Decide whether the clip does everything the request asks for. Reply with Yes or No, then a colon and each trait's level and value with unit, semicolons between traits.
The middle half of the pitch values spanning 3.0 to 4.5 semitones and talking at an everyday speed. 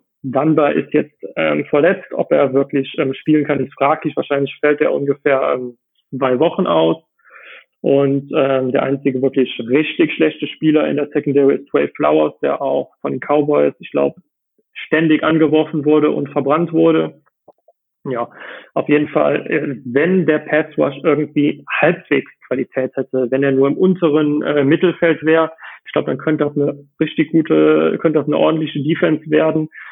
No: narrow, 2.5 semitones; average, 165 wpm